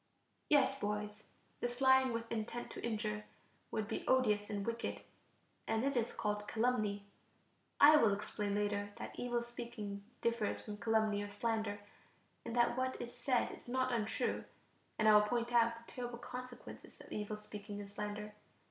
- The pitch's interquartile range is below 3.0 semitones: Yes, narrow, 2.6 semitones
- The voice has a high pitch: Yes, high, 225 Hz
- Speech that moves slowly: No, average, 165 wpm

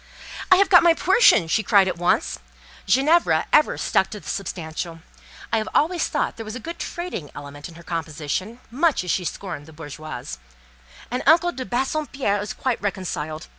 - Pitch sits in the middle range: No, high, 205 Hz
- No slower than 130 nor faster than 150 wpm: No, average, 175 wpm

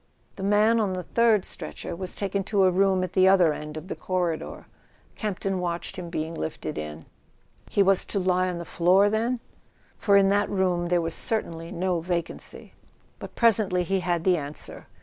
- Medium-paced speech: Yes, average, 190 wpm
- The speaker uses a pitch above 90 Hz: Yes, medium, 185 Hz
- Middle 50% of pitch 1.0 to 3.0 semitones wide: Yes, narrow, 2.5 semitones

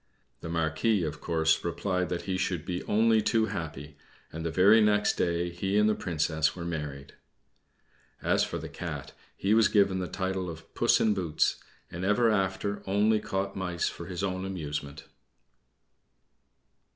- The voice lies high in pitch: No, very low, 90 Hz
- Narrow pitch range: No, average, 3.7 semitones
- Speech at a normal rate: Yes, average, 165 wpm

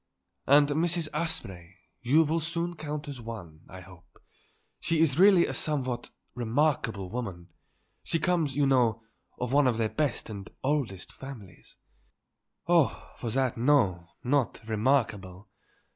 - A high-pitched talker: No, low, 130 Hz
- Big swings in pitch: Yes, wide, 5.8 semitones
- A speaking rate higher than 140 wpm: No, slow, 135 wpm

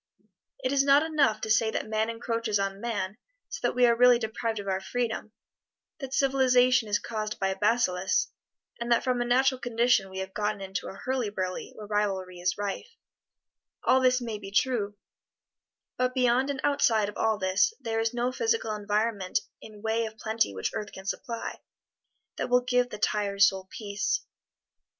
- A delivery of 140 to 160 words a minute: No, average, 180 wpm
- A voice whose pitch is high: Yes, high, 220 Hz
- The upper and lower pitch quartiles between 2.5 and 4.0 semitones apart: Yes, average, 3.4 semitones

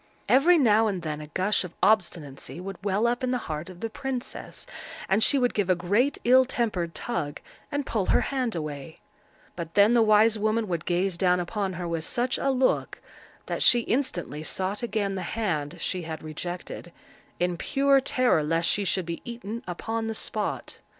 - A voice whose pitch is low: No, high, 200 Hz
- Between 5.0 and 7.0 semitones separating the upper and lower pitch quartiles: Yes, wide, 5.4 semitones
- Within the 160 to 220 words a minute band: Yes, average, 190 wpm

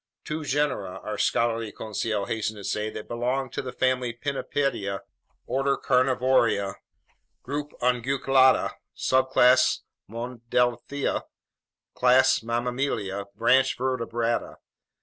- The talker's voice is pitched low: Yes, low, 125 Hz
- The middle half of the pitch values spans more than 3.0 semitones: No, narrow, 2.5 semitones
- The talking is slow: Yes, slow, 95 wpm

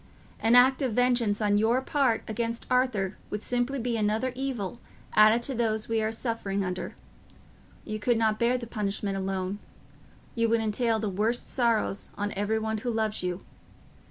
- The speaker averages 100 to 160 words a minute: No, average, 170 wpm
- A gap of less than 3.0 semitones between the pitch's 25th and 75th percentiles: Yes, narrow, 2.6 semitones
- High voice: Yes, high, 225 Hz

